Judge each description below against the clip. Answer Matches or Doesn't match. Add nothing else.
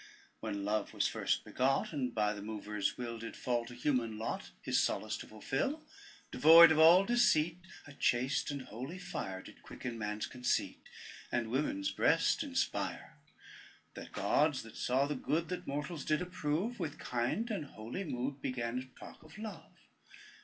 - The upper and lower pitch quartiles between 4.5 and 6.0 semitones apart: Matches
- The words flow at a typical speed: Matches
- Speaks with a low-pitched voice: Matches